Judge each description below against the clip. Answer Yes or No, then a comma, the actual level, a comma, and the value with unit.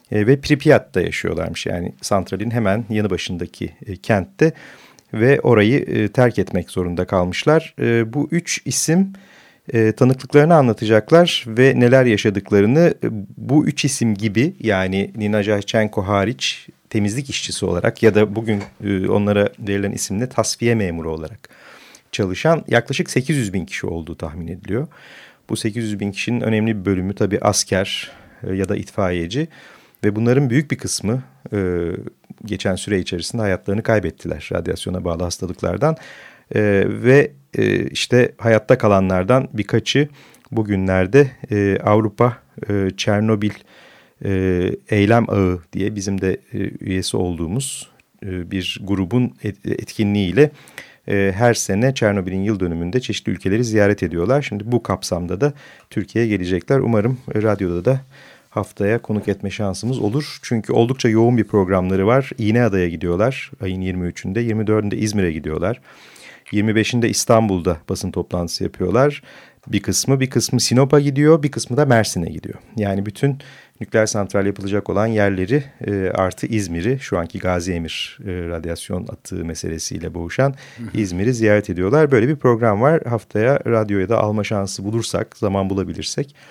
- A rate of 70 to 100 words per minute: No, average, 125 wpm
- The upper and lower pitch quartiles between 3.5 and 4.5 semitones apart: Yes, average, 4.2 semitones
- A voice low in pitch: Yes, low, 105 Hz